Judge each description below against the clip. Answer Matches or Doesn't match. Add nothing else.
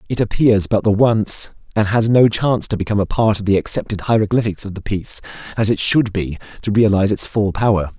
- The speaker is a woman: Doesn't match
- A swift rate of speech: Matches